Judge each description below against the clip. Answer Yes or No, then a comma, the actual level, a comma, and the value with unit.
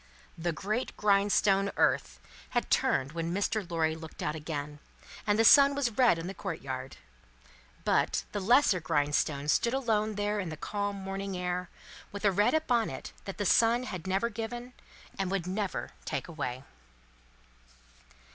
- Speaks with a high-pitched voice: Yes, high, 195 Hz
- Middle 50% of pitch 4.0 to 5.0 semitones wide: Yes, average, 4.7 semitones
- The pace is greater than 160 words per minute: No, average, 155 wpm